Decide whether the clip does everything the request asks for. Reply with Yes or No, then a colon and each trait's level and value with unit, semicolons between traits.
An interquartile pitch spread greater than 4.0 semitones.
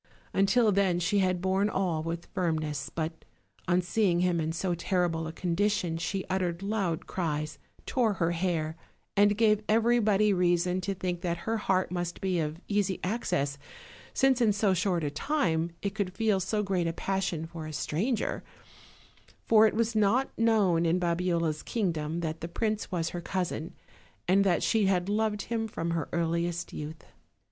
No: average, 3.6 semitones